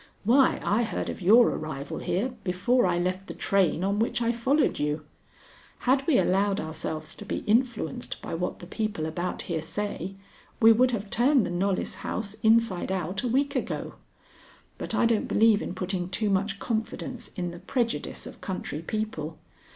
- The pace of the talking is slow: No, average, 175 wpm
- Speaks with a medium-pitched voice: No, high, 200 Hz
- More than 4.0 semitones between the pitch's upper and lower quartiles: Yes, average, 4.5 semitones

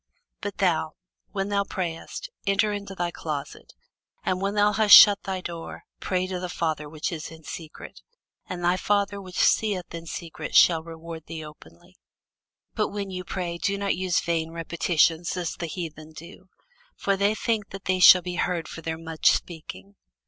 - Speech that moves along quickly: No, average, 175 wpm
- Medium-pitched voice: Yes, medium, 175 Hz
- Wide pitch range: No, average, 3.1 semitones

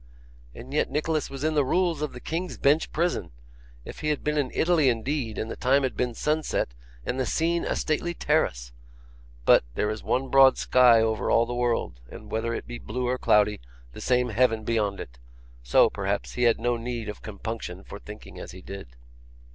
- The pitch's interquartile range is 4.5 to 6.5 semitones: Yes, average, 5.0 semitones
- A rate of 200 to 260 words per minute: Yes, fast, 205 wpm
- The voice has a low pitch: Yes, low, 125 Hz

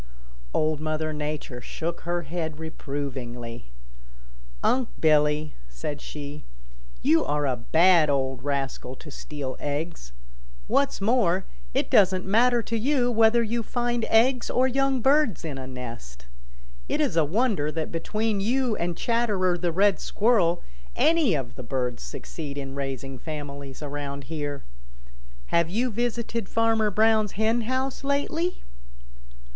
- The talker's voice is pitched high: No, medium, 170 Hz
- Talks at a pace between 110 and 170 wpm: Yes, average, 140 wpm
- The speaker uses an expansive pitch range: Yes, wide, 8.0 semitones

